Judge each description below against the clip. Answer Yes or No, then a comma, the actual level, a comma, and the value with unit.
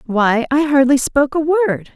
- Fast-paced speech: No, average, 185 wpm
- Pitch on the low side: No, very high, 275 Hz